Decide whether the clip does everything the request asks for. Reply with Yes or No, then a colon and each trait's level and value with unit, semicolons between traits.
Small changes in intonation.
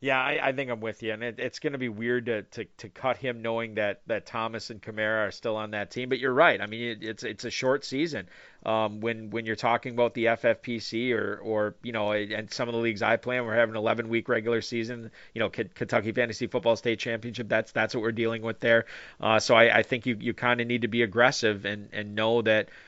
Yes: narrow, 1.6 semitones